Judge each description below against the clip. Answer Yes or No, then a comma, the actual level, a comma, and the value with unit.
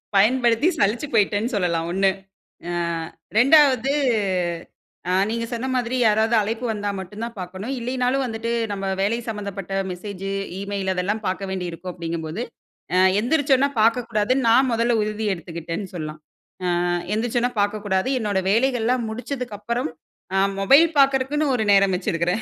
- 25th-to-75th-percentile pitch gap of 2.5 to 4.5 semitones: Yes, average, 4.1 semitones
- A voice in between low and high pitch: No, high, 215 Hz